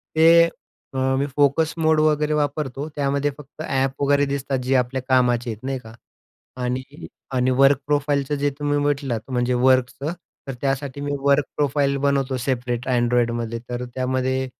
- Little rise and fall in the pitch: Yes, narrow, 2.1 semitones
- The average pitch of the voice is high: No, low, 135 Hz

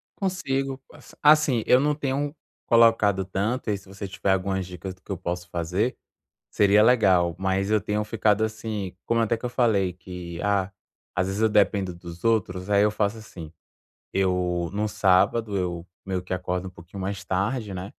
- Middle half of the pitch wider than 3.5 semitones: No, average, 3.2 semitones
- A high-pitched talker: No, low, 100 Hz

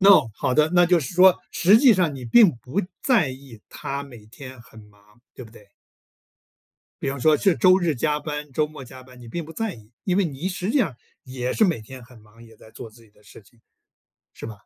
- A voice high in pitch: No, medium, 140 Hz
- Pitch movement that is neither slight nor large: No, wide, 7.0 semitones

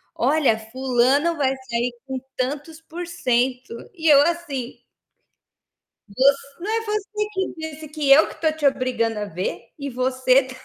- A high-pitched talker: Yes, very high, 275 Hz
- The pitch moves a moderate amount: Yes, average, 4.0 semitones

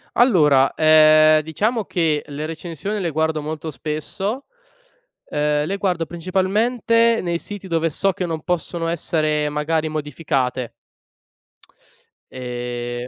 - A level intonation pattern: No, average, 3.6 semitones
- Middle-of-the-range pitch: Yes, medium, 160 Hz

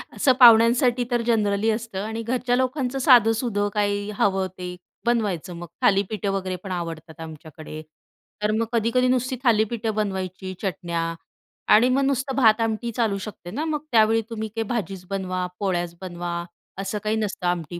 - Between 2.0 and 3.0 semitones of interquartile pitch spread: No, average, 4.2 semitones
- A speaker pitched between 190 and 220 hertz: Yes, high, 210 Hz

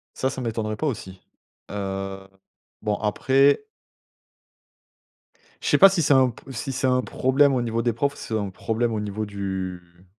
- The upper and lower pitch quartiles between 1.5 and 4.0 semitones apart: No, average, 4.9 semitones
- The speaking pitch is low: Yes, low, 110 Hz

